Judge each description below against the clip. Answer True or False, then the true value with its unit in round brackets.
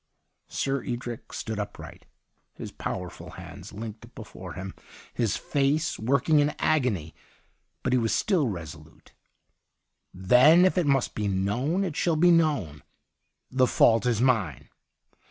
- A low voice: True (125 Hz)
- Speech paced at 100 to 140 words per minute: True (135 wpm)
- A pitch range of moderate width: False (6.4 semitones)